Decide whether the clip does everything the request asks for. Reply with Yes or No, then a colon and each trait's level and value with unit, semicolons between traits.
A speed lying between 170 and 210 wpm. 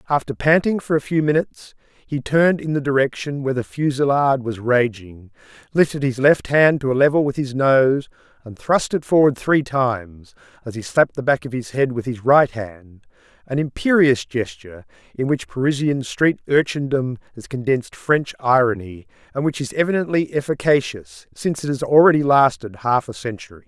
Yes: average, 175 wpm